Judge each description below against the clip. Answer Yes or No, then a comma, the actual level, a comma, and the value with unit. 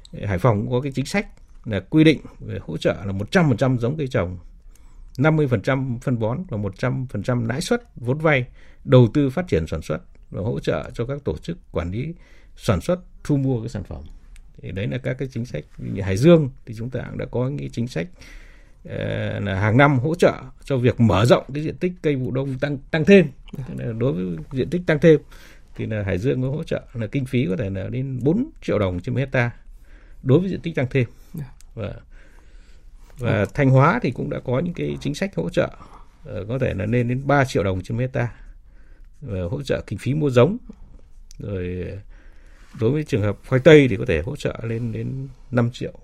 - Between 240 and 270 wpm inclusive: No, average, 210 wpm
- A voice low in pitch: Yes, low, 125 Hz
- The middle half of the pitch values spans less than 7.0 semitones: Yes, wide, 5.6 semitones